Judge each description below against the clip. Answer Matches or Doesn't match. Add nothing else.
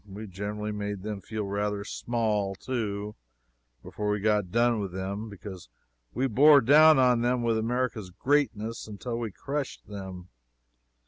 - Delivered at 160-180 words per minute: Doesn't match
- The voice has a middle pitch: Doesn't match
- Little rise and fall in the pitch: Doesn't match